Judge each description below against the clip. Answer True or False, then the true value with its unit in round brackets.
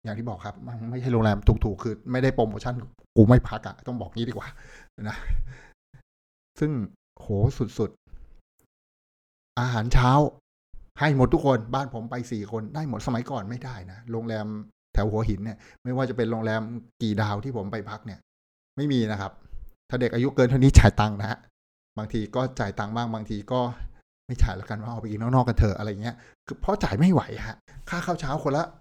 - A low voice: True (115 Hz)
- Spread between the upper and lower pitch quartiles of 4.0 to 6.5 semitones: False (3.0 semitones)